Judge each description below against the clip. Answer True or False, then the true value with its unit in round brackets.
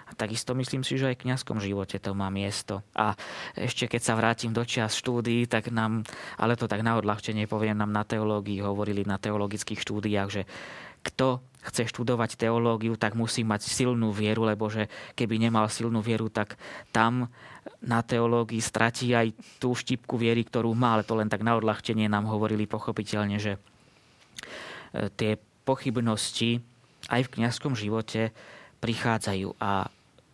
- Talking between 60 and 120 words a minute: False (155 wpm)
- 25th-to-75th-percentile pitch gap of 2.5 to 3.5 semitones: False (2.0 semitones)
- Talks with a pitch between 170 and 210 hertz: False (115 Hz)